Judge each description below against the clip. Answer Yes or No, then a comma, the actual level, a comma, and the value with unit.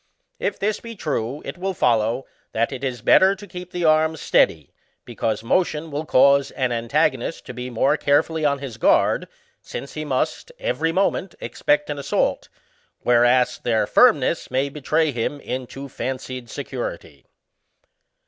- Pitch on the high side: No, medium, 140 Hz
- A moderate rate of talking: Yes, average, 150 wpm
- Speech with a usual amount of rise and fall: Yes, average, 4.7 semitones